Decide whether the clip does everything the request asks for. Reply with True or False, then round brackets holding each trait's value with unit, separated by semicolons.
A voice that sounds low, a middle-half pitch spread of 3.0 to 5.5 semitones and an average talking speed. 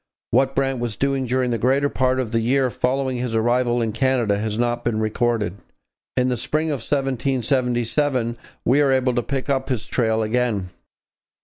False (125 Hz; 2.4 semitones; 180 wpm)